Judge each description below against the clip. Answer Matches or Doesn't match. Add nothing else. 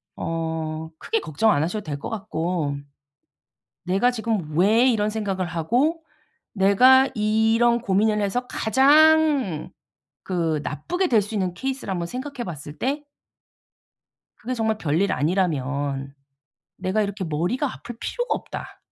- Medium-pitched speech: Doesn't match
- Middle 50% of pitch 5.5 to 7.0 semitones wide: Matches